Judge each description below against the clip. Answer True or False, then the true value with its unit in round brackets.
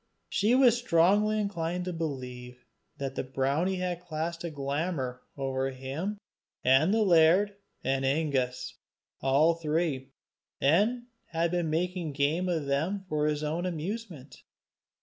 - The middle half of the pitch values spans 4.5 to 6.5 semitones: True (4.8 semitones)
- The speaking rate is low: True (130 wpm)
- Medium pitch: True (160 Hz)